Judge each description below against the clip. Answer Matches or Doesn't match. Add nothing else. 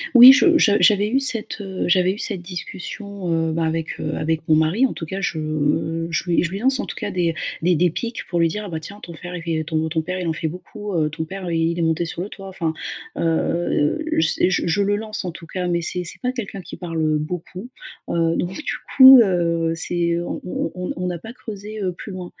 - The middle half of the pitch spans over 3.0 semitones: Matches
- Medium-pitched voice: Matches